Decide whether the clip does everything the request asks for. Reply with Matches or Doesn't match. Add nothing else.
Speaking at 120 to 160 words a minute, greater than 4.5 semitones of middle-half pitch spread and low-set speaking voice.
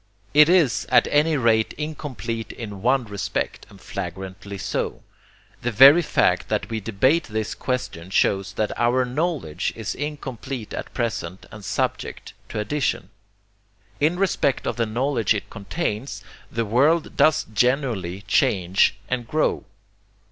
Matches